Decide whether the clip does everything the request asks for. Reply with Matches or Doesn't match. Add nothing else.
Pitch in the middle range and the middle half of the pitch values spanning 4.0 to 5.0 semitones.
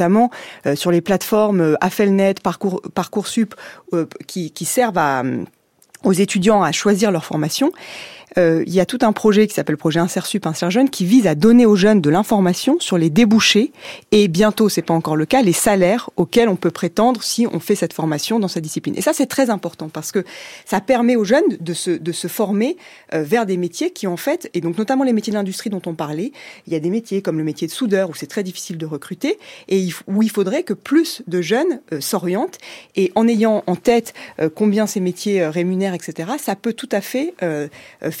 Doesn't match